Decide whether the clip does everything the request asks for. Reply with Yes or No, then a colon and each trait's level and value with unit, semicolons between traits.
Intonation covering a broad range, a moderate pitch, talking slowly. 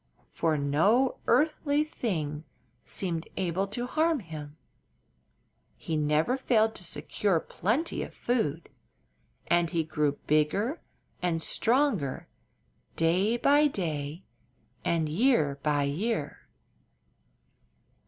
Yes: wide, 7.7 semitones; medium, 175 Hz; slow, 100 wpm